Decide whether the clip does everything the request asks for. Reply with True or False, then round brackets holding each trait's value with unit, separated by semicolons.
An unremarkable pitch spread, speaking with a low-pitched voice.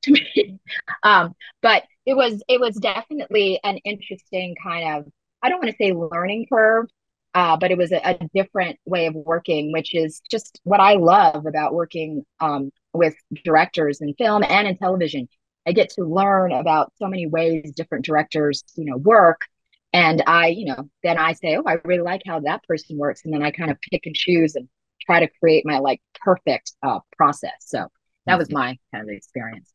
False (4.0 semitones; 170 Hz)